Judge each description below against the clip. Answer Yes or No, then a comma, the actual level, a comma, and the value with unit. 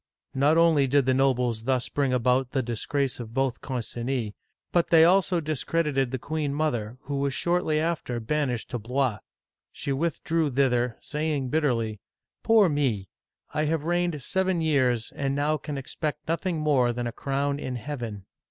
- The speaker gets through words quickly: No, average, 160 wpm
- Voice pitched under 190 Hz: Yes, medium, 140 Hz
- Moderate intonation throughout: Yes, average, 3.8 semitones